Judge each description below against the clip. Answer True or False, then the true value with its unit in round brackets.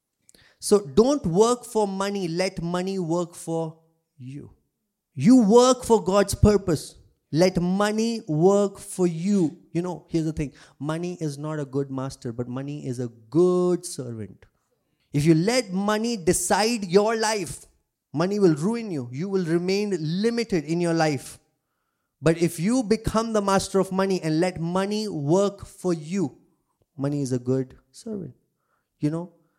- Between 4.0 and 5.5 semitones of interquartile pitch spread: True (4.5 semitones)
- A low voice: False (175 Hz)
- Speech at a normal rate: True (155 wpm)